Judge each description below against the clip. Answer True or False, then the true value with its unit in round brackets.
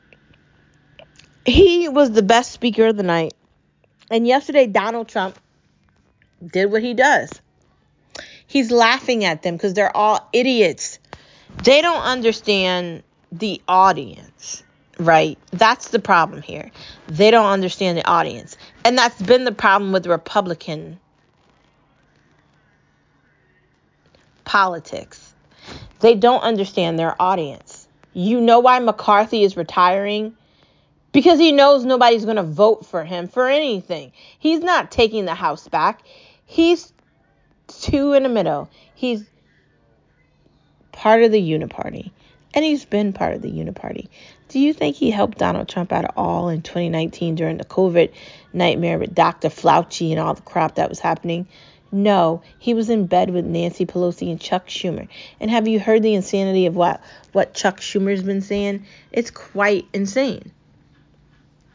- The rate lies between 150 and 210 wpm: False (140 wpm)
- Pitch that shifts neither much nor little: True (5.0 semitones)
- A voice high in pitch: True (205 Hz)